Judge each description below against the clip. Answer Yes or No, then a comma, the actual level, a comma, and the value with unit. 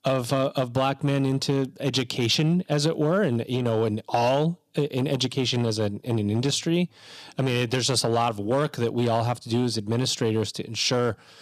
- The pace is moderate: No, fast, 210 wpm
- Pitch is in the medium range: No, low, 130 Hz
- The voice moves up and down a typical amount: Yes, average, 3.0 semitones